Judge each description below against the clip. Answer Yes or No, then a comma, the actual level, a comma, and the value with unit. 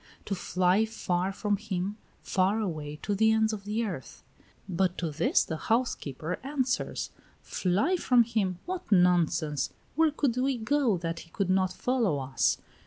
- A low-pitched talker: No, high, 195 Hz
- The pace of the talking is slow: No, average, 160 wpm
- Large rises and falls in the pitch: No, average, 4.5 semitones